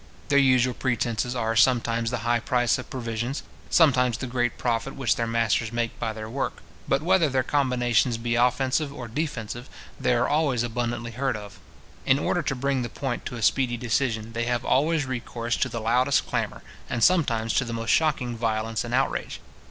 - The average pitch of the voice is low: Yes, low, 120 Hz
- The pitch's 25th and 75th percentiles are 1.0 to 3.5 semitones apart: Yes, narrow, 2.5 semitones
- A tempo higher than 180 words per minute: Yes, average, 190 wpm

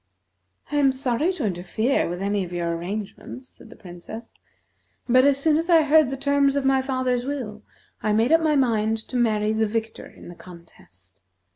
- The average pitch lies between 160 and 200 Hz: No, high, 235 Hz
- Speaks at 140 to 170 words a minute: No, average, 190 wpm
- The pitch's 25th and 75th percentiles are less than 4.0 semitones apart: No, average, 5.2 semitones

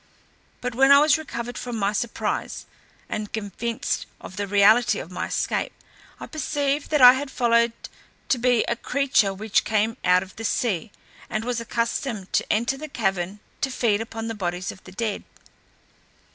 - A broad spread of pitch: No, average, 3.5 semitones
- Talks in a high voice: Yes, high, 230 Hz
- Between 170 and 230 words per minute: Yes, average, 175 wpm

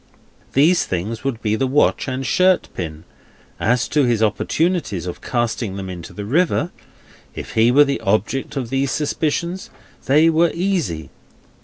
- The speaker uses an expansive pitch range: Yes, wide, 6.4 semitones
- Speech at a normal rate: Yes, average, 155 wpm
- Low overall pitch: Yes, low, 130 Hz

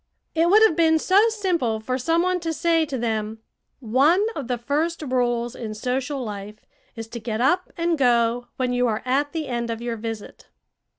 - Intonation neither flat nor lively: No, wide, 5.9 semitones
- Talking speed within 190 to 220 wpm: Yes, average, 195 wpm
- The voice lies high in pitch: Yes, very high, 255 Hz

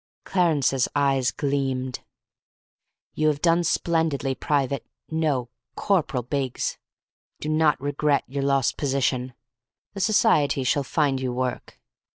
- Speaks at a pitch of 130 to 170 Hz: Yes, medium, 140 Hz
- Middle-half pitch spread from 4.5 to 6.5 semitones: No, average, 2.8 semitones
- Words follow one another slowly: Yes, slow, 115 wpm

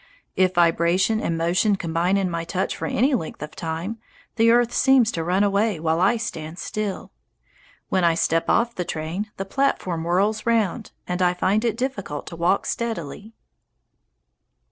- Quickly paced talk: No, average, 165 wpm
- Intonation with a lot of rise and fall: No, average, 4.6 semitones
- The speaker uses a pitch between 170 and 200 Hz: Yes, medium, 185 Hz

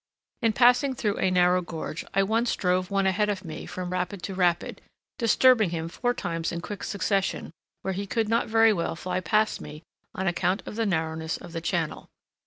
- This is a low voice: No, high, 190 Hz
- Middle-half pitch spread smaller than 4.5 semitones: Yes, average, 3.7 semitones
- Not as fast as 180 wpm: No, average, 195 wpm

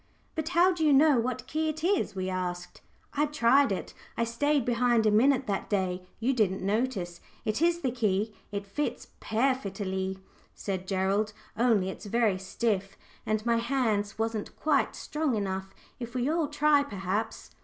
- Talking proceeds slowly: No, average, 165 wpm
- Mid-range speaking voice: No, high, 230 Hz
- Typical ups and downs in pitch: No, wide, 5.8 semitones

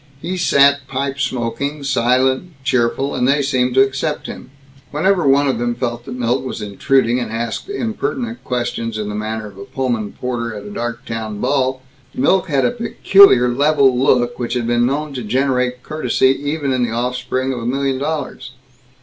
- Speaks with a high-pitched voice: No, low, 130 Hz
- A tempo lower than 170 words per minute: No, average, 180 wpm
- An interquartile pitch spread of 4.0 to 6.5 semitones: No, average, 2.8 semitones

